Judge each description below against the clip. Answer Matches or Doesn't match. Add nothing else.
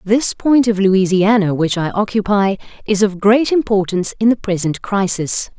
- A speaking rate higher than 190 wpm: Doesn't match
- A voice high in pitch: Matches